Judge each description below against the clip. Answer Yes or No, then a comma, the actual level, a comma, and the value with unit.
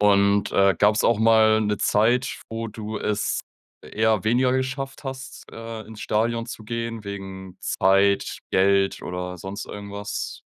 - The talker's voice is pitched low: Yes, low, 105 Hz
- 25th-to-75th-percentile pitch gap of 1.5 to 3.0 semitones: Yes, narrow, 2.4 semitones